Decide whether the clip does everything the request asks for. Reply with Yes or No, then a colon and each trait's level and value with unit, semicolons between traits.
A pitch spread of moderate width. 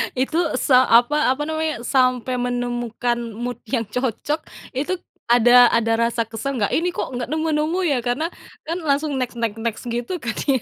Yes: average, 3.9 semitones